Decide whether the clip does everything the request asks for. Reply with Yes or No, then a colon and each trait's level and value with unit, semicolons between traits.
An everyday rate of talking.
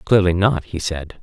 Yes: average, 195 wpm